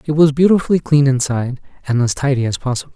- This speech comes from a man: Yes, male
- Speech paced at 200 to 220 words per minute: Yes, fast, 205 wpm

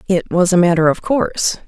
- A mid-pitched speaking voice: Yes, medium, 180 Hz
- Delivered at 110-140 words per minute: No, fast, 215 wpm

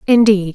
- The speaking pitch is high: Yes, high, 205 Hz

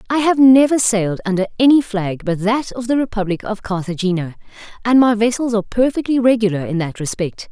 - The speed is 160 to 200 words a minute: Yes, average, 185 wpm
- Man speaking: No, female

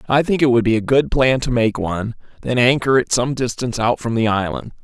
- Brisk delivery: Yes, fast, 250 wpm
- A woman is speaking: No, male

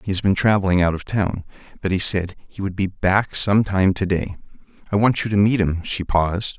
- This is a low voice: Yes, very low, 95 Hz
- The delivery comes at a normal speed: No, fast, 235 wpm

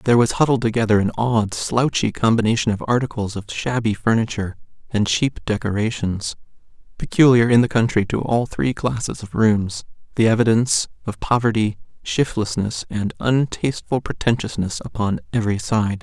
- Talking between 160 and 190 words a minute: No, average, 140 wpm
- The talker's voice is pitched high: No, low, 110 Hz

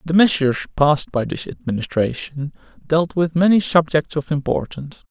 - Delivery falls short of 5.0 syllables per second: No, 5.3 syllables/s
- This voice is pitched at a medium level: Yes, medium, 150 Hz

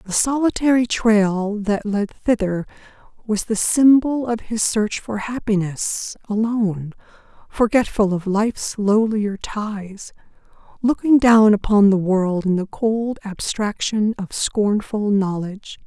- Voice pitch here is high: Yes, high, 215 Hz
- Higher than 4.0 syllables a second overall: No, 3.8 syllables/s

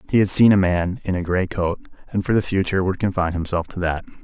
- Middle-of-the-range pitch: No, very low, 95 Hz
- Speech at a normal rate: No, fast, 255 wpm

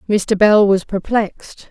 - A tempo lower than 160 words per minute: Yes, average, 140 wpm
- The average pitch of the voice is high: Yes, high, 205 Hz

